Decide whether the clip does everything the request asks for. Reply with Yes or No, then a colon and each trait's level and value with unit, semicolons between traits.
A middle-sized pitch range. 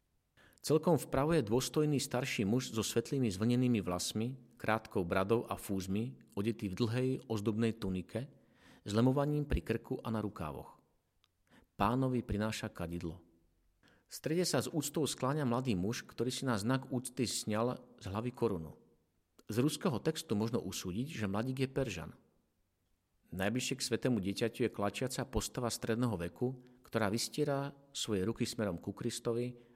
Yes: average, 3.9 semitones